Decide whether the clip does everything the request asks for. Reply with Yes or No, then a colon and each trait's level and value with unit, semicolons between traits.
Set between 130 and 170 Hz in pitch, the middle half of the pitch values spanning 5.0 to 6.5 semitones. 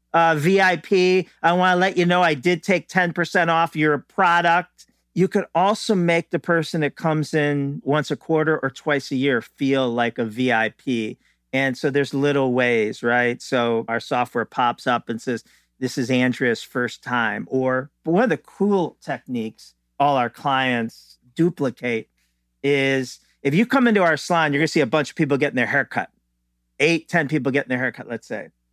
Yes: medium, 140 Hz; average, 5.3 semitones